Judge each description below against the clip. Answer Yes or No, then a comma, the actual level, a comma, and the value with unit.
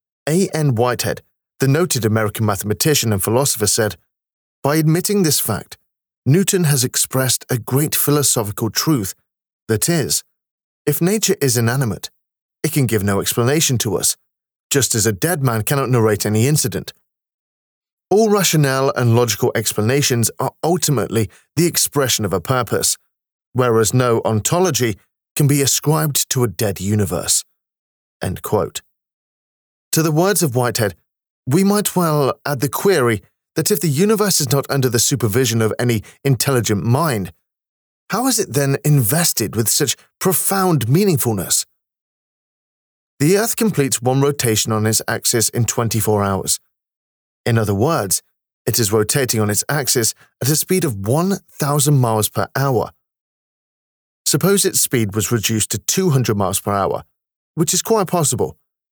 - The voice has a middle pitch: No, low, 125 Hz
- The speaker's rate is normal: Yes, average, 145 wpm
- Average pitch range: No, wide, 5.8 semitones